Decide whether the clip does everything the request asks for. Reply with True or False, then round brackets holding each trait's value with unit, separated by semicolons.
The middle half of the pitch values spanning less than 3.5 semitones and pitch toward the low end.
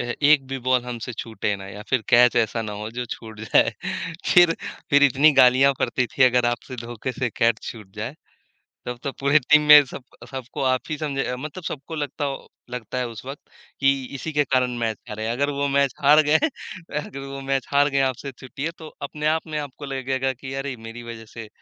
True (3.1 semitones; 130 Hz)